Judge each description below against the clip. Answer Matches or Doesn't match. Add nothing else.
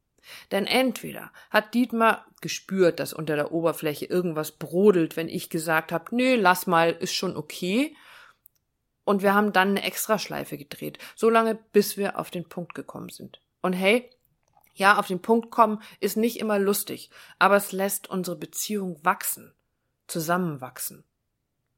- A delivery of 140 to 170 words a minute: Matches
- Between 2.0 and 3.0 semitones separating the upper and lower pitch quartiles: Doesn't match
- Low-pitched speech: Doesn't match